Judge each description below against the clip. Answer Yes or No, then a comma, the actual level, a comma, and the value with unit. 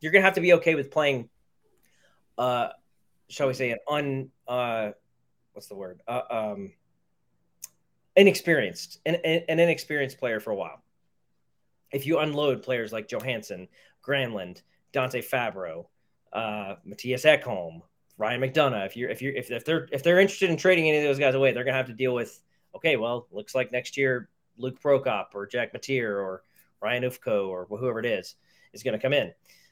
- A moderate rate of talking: Yes, average, 175 wpm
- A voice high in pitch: No, low, 130 Hz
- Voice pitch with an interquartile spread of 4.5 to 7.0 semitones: Yes, wide, 5.5 semitones